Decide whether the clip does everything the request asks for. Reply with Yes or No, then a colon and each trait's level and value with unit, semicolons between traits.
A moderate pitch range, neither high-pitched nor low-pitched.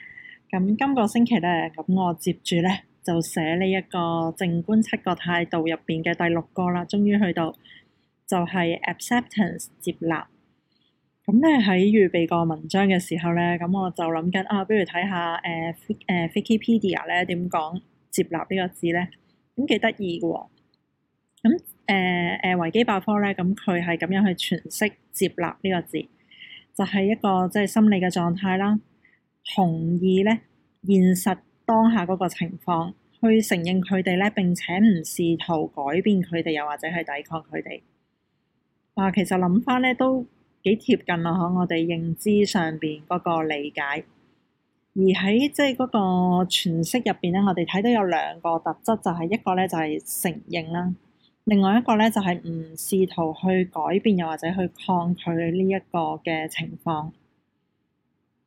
Yes: average, 3.1 semitones; medium, 180 Hz